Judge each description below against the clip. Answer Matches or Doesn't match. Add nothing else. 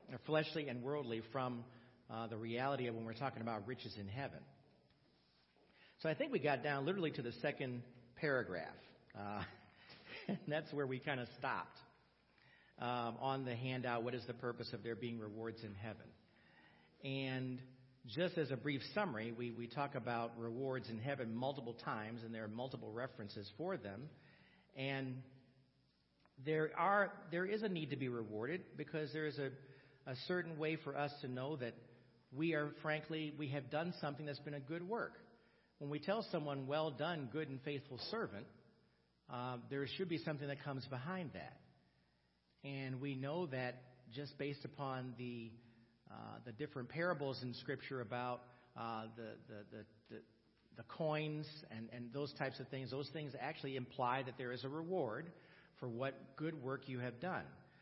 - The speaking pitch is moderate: Doesn't match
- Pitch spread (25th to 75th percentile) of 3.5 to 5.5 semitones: Matches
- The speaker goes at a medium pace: Matches